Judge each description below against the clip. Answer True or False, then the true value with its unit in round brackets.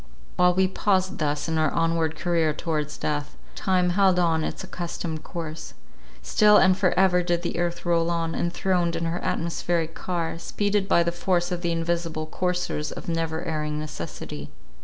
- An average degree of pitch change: False (1.8 semitones)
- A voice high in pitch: False (170 Hz)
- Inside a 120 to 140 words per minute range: False (170 wpm)